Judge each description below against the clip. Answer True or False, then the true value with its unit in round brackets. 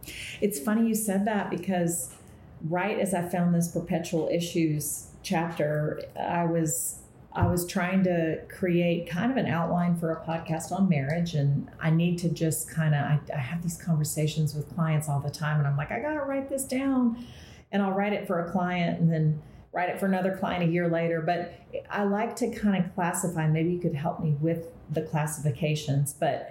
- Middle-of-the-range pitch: True (170 Hz)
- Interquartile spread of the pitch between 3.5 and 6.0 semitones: False (2.8 semitones)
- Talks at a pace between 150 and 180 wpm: False (200 wpm)